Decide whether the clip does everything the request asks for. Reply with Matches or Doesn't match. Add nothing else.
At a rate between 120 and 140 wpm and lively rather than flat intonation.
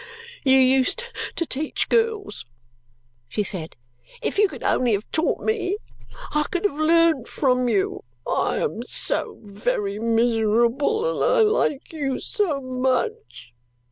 Matches